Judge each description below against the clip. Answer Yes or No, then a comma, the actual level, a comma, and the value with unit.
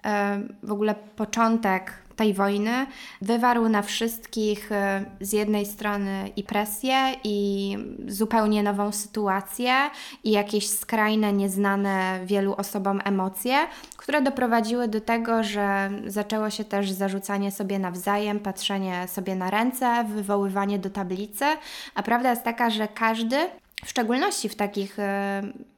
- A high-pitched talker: Yes, high, 210 Hz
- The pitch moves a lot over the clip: No, average, 2.8 semitones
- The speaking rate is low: No, average, 120 wpm